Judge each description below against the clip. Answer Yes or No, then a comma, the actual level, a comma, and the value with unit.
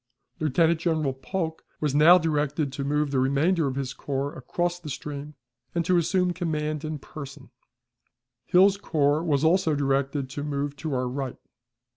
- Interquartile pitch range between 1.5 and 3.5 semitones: Yes, average, 2.9 semitones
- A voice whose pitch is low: No, medium, 150 Hz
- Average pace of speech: Yes, average, 160 wpm